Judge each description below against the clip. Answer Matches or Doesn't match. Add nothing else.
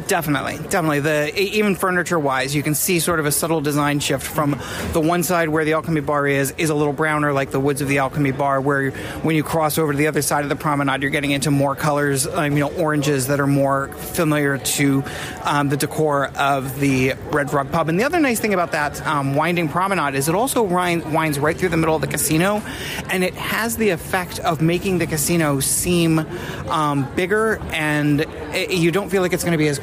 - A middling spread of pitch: Matches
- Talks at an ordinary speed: Doesn't match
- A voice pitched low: Doesn't match